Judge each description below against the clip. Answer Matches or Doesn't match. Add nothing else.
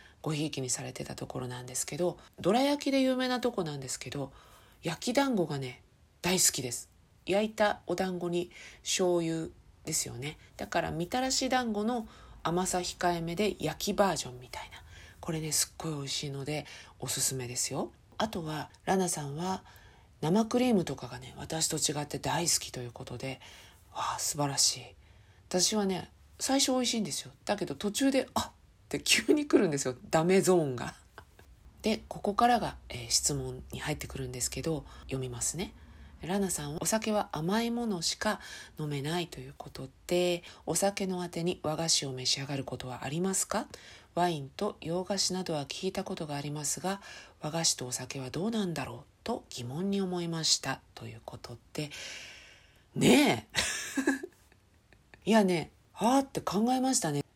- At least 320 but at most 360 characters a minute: Matches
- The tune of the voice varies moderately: Doesn't match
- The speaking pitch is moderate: Matches